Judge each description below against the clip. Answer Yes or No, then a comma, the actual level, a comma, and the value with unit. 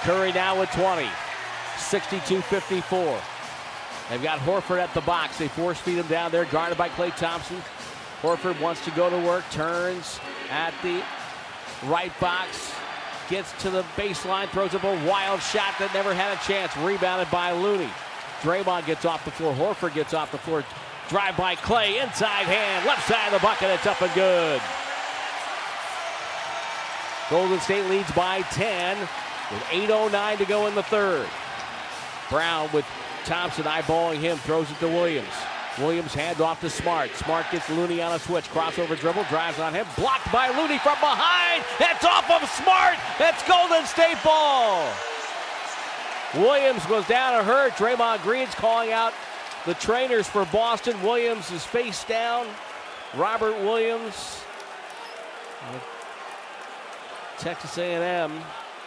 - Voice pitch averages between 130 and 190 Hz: Yes, medium, 185 Hz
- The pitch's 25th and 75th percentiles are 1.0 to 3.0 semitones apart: No, average, 4.9 semitones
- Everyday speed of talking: Yes, average, 145 wpm